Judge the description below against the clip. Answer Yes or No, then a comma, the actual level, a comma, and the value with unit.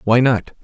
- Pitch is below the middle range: Yes, low, 120 Hz